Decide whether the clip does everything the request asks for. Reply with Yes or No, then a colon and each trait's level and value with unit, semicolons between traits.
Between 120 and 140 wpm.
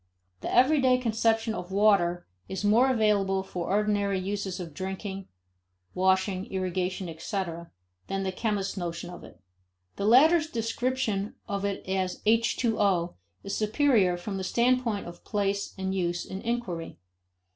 Yes: slow, 135 wpm